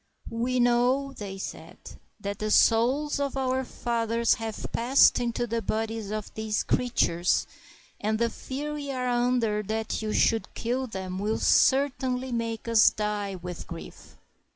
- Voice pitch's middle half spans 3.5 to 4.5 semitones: No, average, 2.9 semitones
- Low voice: No, high, 230 Hz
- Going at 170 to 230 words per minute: No, average, 155 wpm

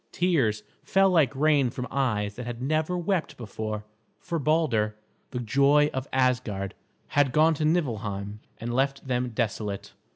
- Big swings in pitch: Yes, wide, 5.9 semitones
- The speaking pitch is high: No, low, 130 Hz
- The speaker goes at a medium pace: Yes, average, 150 wpm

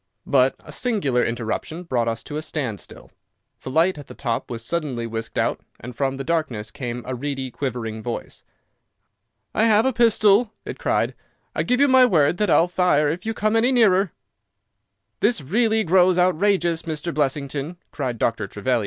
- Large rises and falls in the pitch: Yes, wide, 7.6 semitones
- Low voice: No, medium, 155 Hz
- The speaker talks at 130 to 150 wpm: No, average, 175 wpm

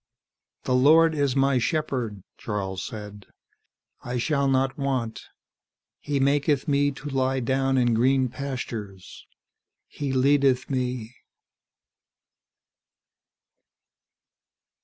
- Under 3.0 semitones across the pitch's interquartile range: Yes, narrow, 2.5 semitones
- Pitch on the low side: Yes, low, 130 Hz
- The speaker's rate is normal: No, slow, 95 wpm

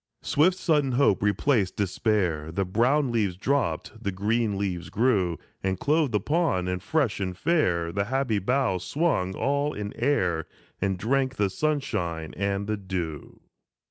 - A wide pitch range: Yes, wide, 6.7 semitones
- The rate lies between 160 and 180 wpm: No, average, 145 wpm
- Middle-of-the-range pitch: No, low, 105 Hz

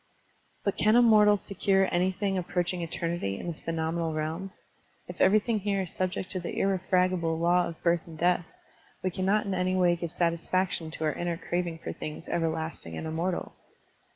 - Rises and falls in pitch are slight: Yes, narrow, 2.3 semitones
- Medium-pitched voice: Yes, medium, 175 Hz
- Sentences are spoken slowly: No, average, 180 wpm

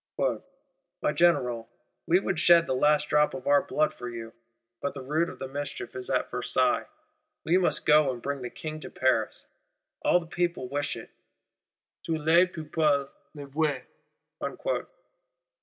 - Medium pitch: Yes, medium, 150 Hz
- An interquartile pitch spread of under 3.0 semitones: No, average, 4.0 semitones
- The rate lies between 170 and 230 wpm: No, average, 155 wpm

